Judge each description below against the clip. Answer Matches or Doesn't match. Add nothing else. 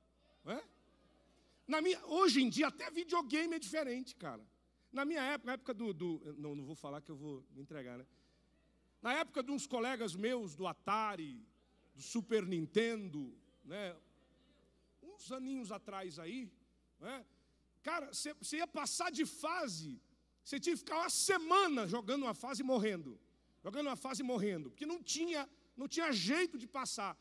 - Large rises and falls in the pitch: Matches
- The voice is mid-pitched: Doesn't match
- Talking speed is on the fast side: Doesn't match